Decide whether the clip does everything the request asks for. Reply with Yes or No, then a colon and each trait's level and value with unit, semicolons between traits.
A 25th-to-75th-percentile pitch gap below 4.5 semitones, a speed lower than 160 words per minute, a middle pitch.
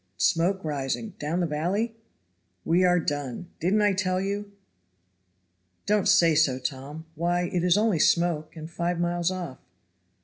Yes: average, 3.3 semitones; average, 145 wpm; medium, 175 Hz